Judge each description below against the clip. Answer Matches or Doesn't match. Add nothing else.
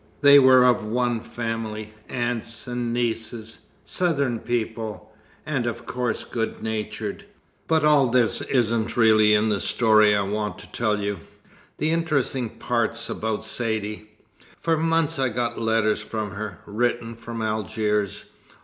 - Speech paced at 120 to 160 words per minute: Matches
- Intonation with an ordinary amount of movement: Doesn't match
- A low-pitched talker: Matches